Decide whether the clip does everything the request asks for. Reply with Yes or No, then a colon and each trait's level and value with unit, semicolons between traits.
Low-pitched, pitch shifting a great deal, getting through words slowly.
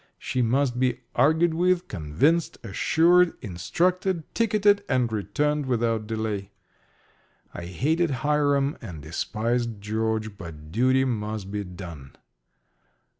Yes: low, 120 Hz; wide, 6.6 semitones; slow, 110 wpm